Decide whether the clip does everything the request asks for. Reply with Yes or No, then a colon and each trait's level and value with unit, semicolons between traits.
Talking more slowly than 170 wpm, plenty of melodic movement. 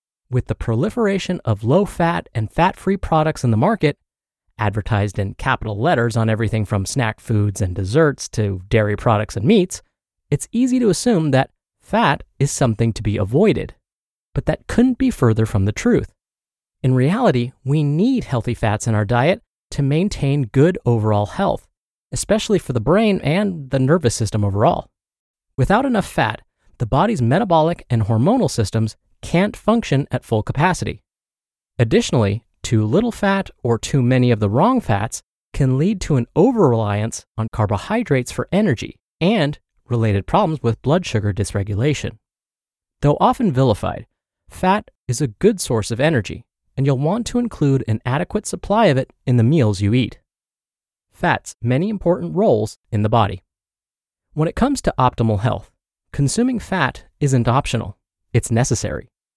Yes: average, 160 wpm; wide, 7.6 semitones